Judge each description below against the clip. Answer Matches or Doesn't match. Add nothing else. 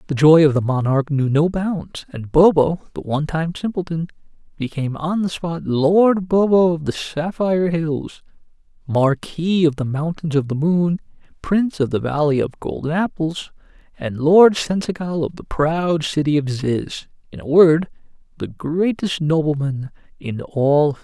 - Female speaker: Doesn't match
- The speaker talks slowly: Doesn't match